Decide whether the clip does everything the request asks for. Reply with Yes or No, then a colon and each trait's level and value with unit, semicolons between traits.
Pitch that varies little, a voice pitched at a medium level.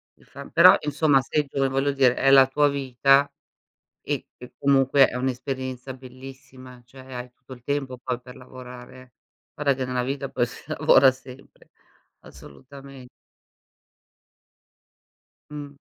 No: narrow, 1.6 semitones; low, 130 Hz